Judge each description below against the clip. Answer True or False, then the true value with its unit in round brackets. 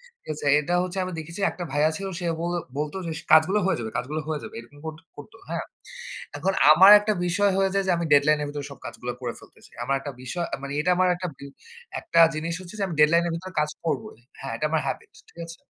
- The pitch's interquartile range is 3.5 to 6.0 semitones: True (3.8 semitones)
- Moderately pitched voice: True (160 Hz)